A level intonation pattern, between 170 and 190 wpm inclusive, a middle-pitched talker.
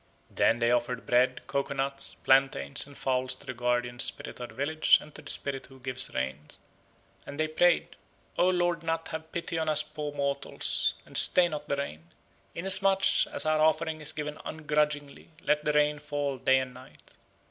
No: average, 3.4 semitones; average, 185 wpm; medium, 145 Hz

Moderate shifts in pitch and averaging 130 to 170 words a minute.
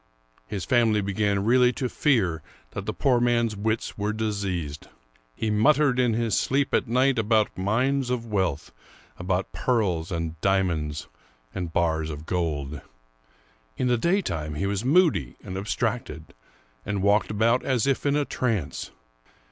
No: wide, 5.7 semitones; average, 150 wpm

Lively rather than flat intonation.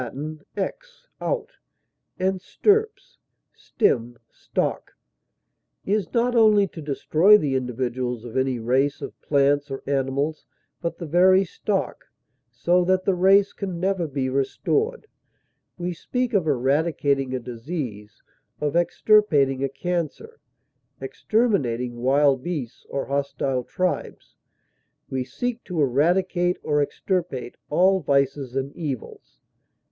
Yes: wide, 6.1 semitones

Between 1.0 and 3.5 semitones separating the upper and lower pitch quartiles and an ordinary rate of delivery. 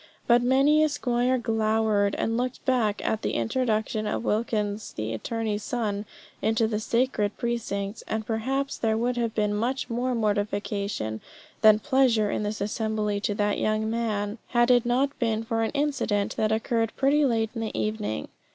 Yes: narrow, 2.5 semitones; average, 170 wpm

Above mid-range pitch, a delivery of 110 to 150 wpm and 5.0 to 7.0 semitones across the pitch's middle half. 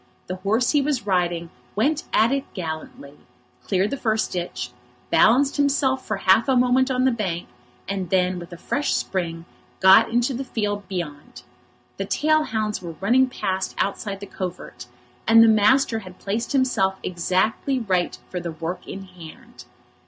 No: high, 205 Hz; average, 165 wpm; wide, 5.6 semitones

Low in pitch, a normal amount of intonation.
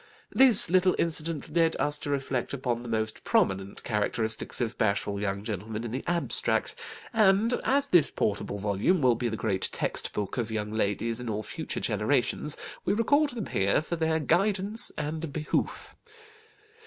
No: low, 130 Hz; wide, 8.1 semitones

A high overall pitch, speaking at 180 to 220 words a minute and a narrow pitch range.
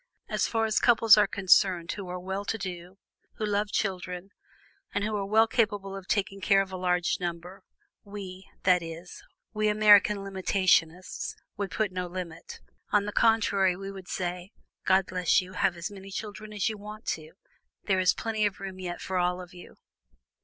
Yes: high, 195 Hz; average, 185 wpm; narrow, 2.3 semitones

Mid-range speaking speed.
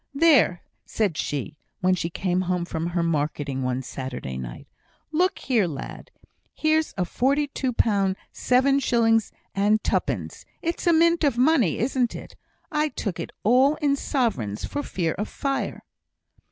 Yes: average, 150 wpm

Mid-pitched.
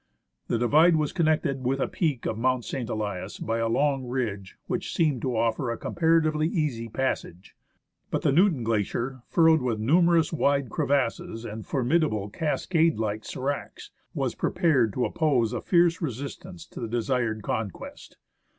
No: low, 130 Hz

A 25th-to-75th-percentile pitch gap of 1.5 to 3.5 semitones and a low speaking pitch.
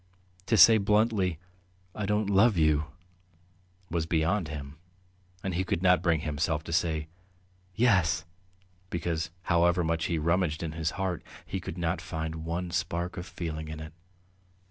Yes: average, 2.7 semitones; very low, 85 Hz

